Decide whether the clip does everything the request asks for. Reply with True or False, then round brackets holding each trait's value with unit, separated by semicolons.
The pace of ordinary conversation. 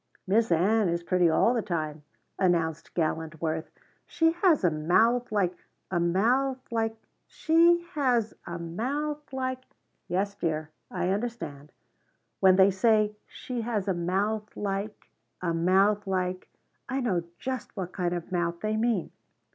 True (150 wpm)